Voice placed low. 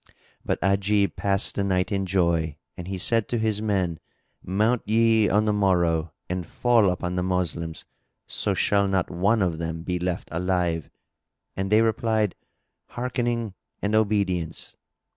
Yes: very low, 95 Hz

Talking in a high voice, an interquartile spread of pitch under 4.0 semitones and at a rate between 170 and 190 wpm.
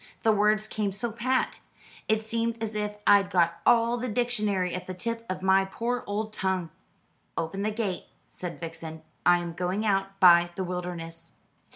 Yes: high, 195 Hz; average, 3.5 semitones; average, 175 wpm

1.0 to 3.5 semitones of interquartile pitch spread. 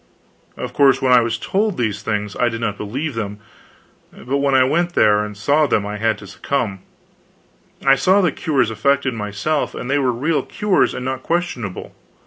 No: average, 5.2 semitones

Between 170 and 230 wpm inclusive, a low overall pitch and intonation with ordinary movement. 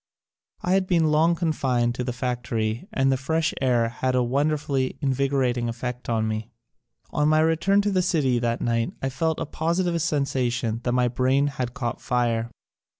Yes: average, 175 wpm; low, 130 Hz; average, 4.4 semitones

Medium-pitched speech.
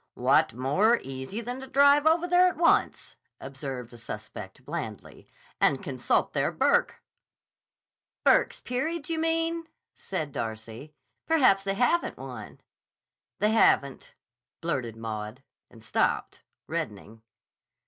Yes: medium, 155 Hz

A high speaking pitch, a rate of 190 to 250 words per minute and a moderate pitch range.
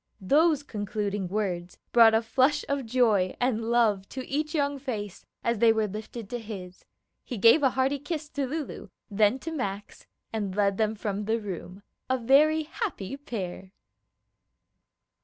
No: high, 225 Hz; average, 155 wpm; average, 5.0 semitones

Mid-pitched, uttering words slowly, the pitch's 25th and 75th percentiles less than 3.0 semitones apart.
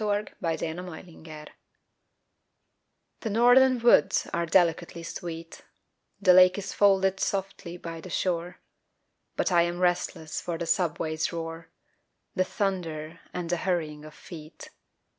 Yes: medium, 175 Hz; slow, 125 wpm; narrow, 2.6 semitones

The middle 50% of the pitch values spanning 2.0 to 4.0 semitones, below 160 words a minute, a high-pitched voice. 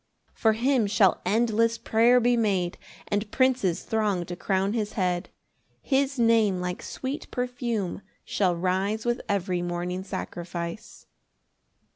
No: average, 4.4 semitones; slow, 135 wpm; high, 210 Hz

